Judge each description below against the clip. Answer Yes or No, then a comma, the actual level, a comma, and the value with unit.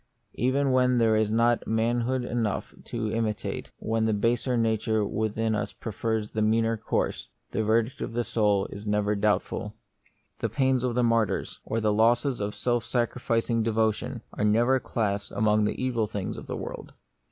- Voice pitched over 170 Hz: No, low, 115 Hz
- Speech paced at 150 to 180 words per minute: Yes, average, 170 wpm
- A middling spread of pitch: No, narrow, 2.0 semitones